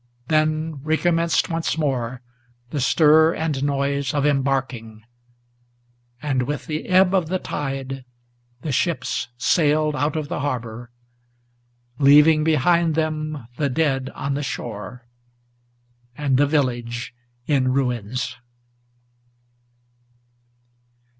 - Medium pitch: Yes, medium, 145 Hz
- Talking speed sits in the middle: No, slow, 105 wpm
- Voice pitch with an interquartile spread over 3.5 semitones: No, average, 3.2 semitones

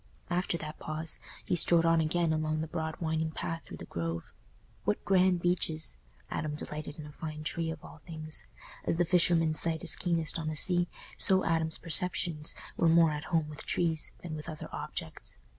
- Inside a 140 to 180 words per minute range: No, average, 190 wpm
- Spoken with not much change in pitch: Yes, narrow, 1.6 semitones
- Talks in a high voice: No, medium, 160 Hz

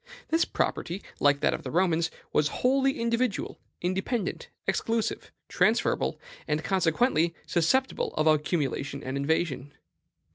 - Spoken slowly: Yes, slow, 115 wpm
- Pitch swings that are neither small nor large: No, wide, 7.3 semitones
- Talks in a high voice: No, medium, 170 Hz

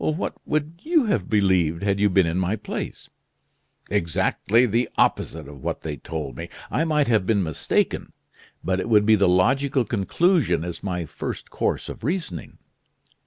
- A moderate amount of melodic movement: No, wide, 6.7 semitones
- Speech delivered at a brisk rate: No, average, 165 wpm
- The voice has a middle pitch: No, low, 100 Hz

